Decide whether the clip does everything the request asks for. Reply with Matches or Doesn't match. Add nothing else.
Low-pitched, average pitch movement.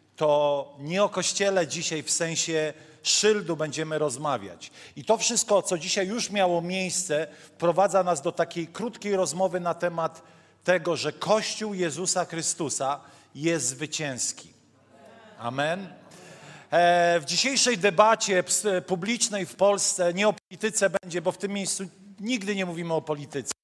Doesn't match